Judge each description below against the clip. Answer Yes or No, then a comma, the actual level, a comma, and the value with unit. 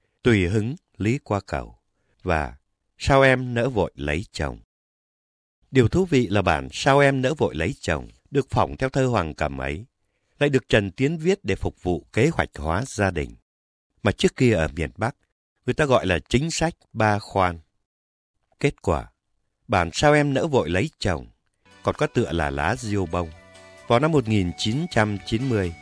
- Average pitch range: No, wide, 7.5 semitones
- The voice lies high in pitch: No, low, 100 Hz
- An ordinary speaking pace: Yes, average, 175 wpm